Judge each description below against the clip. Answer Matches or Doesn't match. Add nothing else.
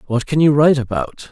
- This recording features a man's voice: Matches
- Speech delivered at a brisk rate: Matches